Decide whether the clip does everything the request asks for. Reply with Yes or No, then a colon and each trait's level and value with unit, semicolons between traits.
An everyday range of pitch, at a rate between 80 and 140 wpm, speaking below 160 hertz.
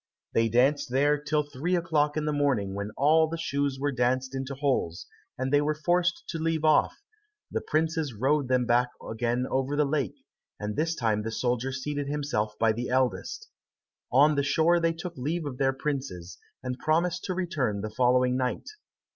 No: average, 3.6 semitones; average, 185 wpm; medium, 140 Hz